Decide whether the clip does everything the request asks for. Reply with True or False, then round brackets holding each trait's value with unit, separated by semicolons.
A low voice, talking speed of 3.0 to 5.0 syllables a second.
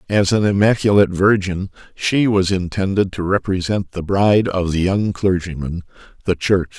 True (95 Hz; 4.9 syllables/s)